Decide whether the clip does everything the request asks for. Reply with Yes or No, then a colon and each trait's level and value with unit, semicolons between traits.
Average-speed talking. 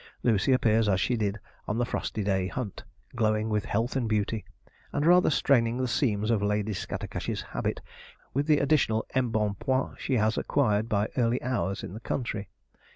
Yes: average, 170 wpm